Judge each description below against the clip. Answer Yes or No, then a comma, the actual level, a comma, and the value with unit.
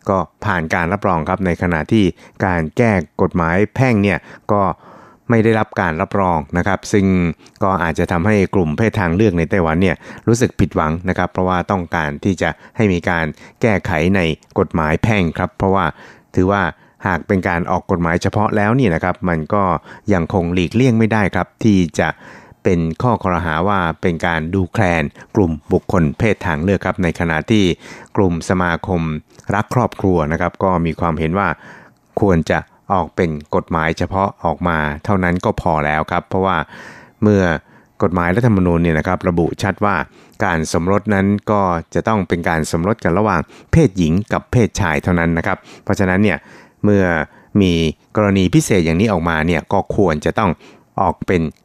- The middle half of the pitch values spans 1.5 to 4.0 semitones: Yes, average, 3.3 semitones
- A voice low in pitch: Yes, very low, 90 Hz